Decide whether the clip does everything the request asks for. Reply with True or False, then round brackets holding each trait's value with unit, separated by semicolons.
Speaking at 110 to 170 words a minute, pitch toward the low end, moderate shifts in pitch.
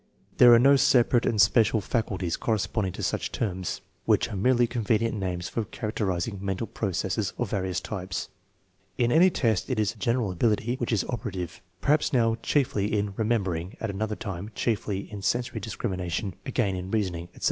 False (185 wpm; 105 Hz; 3.8 semitones)